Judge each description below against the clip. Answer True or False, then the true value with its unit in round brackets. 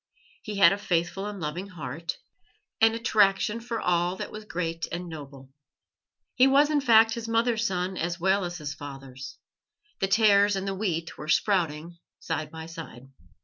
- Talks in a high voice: False (180 Hz)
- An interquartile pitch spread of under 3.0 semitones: False (4.6 semitones)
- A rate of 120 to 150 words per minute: False (170 wpm)